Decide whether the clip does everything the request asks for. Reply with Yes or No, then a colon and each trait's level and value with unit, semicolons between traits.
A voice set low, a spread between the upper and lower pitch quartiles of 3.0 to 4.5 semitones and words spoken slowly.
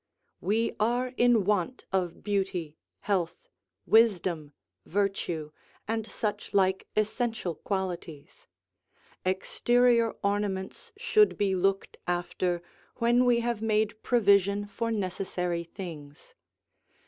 No: high, 200 Hz; average, 3.9 semitones; slow, 100 wpm